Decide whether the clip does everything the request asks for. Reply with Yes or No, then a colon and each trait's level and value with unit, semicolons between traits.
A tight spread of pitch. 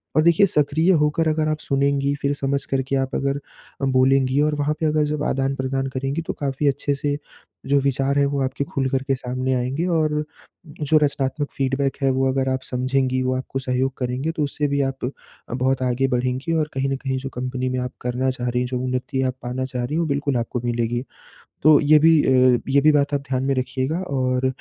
Yes: narrow, 1.9 semitones